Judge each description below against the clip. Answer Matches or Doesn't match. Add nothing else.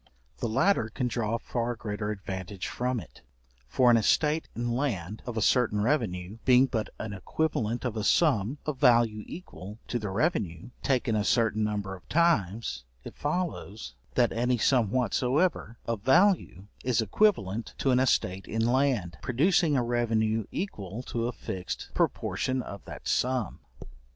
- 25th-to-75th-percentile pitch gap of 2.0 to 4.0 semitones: Matches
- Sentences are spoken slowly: Doesn't match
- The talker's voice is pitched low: Matches